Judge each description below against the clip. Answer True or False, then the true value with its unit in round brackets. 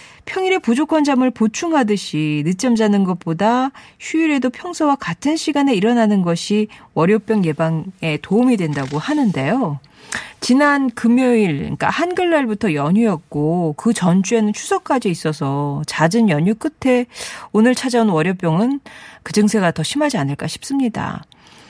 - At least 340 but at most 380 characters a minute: False (315 characters per minute)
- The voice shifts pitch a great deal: True (7.8 semitones)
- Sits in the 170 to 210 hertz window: False (220 Hz)